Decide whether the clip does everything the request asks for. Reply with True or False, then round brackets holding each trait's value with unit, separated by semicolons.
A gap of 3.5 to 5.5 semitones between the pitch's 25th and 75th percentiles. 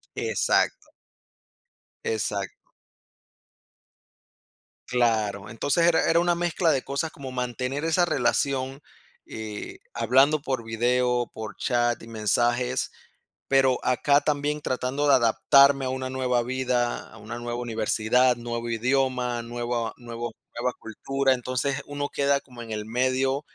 False (2.6 semitones)